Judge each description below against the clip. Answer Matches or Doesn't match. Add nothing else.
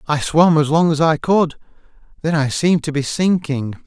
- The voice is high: Doesn't match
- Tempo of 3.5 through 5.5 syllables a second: Matches